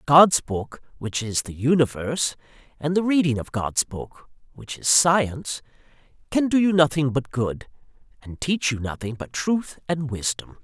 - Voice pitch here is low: No, medium, 145 Hz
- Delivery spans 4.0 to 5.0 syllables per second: Yes, 4.5 syllables/s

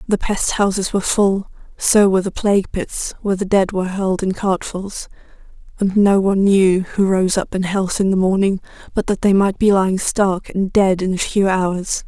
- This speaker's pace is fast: Yes, fast, 210 wpm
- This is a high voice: Yes, high, 195 Hz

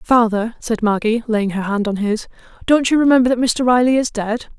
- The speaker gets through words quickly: Yes, fast, 210 wpm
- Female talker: Yes, female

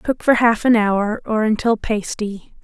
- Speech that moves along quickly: No, average, 180 wpm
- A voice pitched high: Yes, high, 220 Hz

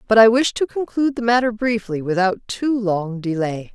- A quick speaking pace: No, average, 190 wpm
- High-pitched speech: Yes, high, 220 Hz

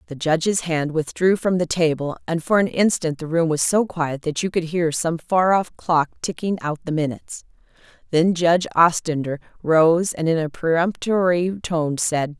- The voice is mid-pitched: Yes, medium, 165 Hz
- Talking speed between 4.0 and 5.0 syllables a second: Yes, 4.7 syllables/s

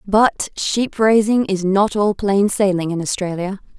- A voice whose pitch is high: Yes, high, 200 Hz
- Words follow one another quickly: No, average, 160 wpm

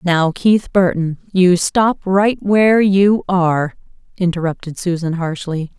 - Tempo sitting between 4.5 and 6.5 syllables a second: No, 4.0 syllables/s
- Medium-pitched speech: Yes, medium, 180 Hz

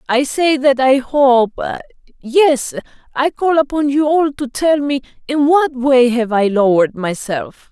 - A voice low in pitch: No, very high, 265 Hz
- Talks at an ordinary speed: Yes, average, 165 wpm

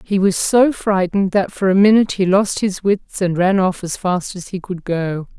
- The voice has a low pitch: No, high, 190 Hz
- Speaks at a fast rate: Yes, fast, 235 wpm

